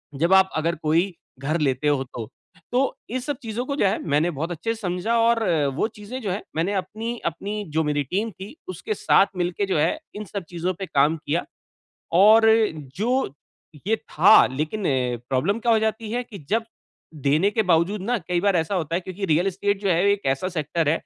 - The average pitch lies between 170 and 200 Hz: Yes, high, 190 Hz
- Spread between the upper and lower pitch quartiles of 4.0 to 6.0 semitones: Yes, average, 4.9 semitones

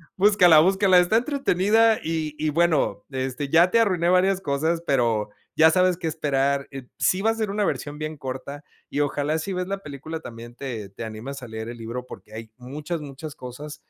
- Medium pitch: Yes, medium, 150 Hz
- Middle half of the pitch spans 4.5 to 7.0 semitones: Yes, wide, 5.5 semitones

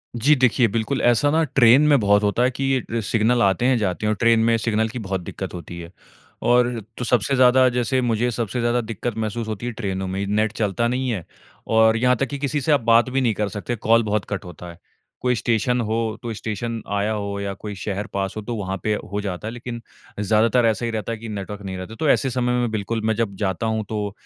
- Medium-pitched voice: No, low, 110 Hz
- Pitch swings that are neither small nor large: Yes, average, 3.0 semitones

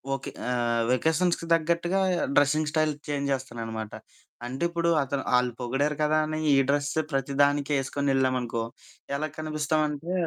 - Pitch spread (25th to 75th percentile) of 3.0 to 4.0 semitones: No, narrow, 2.6 semitones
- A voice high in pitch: No, medium, 145 Hz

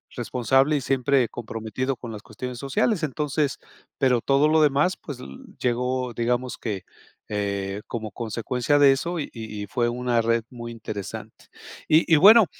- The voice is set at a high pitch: No, low, 125 Hz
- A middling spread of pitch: Yes, average, 3.4 semitones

